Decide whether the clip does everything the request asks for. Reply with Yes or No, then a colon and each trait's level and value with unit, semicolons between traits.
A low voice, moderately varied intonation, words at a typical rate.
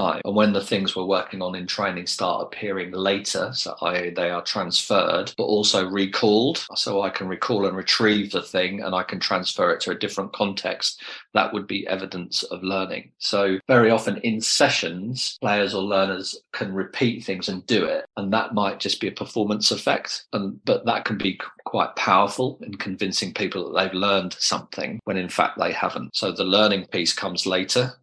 No: low, 100 Hz; narrow, 2.0 semitones; average, 195 wpm